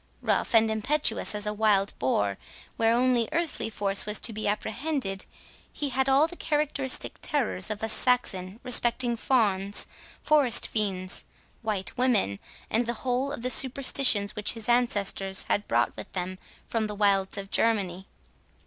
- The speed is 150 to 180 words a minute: Yes, average, 155 wpm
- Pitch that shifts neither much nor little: Yes, average, 4.2 semitones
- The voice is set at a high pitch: Yes, high, 220 Hz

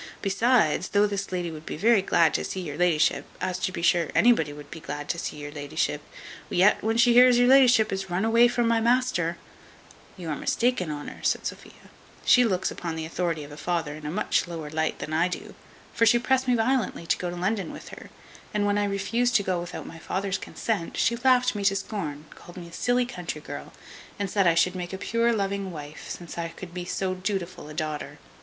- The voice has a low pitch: No, medium, 185 Hz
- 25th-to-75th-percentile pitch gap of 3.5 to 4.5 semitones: No, average, 5.3 semitones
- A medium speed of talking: No, fast, 225 wpm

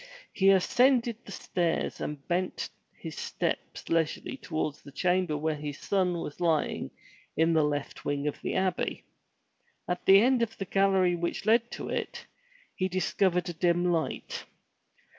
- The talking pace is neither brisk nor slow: Yes, average, 155 wpm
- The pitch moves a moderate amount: Yes, average, 3.5 semitones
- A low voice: No, medium, 180 Hz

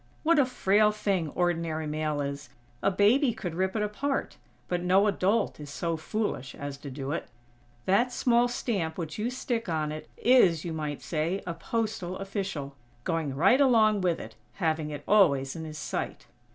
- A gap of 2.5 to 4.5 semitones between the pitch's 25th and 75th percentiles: No, wide, 5.6 semitones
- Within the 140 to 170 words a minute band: No, average, 180 wpm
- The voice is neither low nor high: Yes, medium, 180 Hz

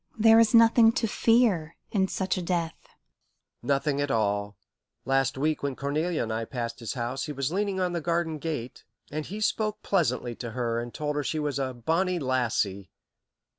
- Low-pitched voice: No, medium, 150 Hz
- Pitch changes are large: Yes, wide, 6.6 semitones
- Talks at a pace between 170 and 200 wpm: Yes, average, 185 wpm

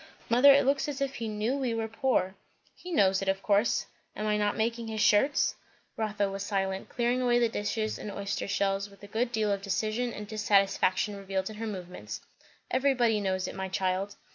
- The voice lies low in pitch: No, high, 210 Hz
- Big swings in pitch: No, average, 3.2 semitones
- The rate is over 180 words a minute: Yes, average, 200 wpm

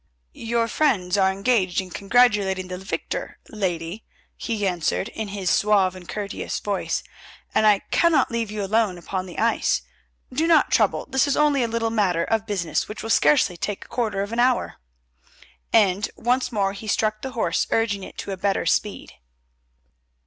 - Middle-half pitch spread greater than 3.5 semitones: No, average, 3.2 semitones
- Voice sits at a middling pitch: No, high, 205 Hz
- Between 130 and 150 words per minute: No, average, 175 wpm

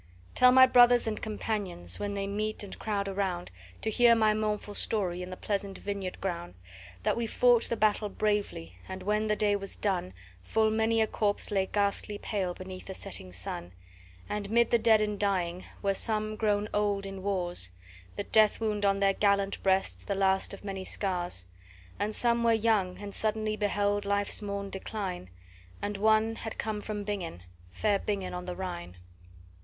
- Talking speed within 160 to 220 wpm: Yes, average, 180 wpm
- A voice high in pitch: Yes, high, 205 Hz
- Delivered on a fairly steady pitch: Yes, narrow, 2.1 semitones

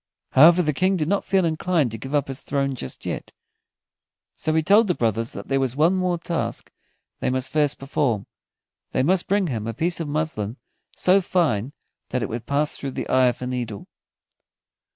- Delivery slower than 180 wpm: No, average, 195 wpm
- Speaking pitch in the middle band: Yes, medium, 145 Hz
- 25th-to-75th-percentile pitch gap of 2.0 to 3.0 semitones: No, average, 5.3 semitones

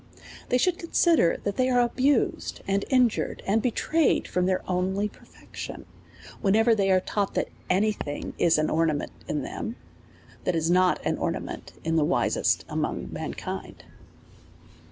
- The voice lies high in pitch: Yes, high, 195 Hz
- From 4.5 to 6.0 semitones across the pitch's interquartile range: Yes, average, 5.1 semitones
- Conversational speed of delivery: Yes, average, 155 wpm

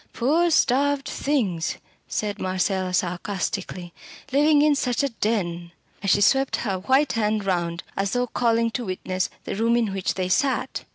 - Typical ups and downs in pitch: No, wide, 5.9 semitones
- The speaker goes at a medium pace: Yes, average, 160 wpm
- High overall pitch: Yes, high, 210 Hz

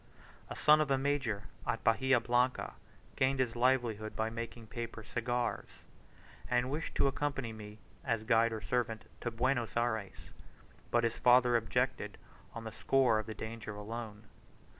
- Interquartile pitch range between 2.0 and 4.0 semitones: Yes, narrow, 2.5 semitones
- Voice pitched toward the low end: Yes, low, 120 Hz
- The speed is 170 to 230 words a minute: No, average, 160 wpm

